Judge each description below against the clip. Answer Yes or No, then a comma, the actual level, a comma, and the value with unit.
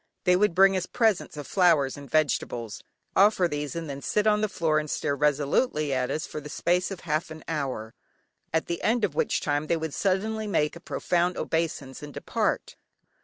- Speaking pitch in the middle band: Yes, medium, 160 Hz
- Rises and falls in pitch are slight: No, average, 4.2 semitones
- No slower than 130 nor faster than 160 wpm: No, average, 200 wpm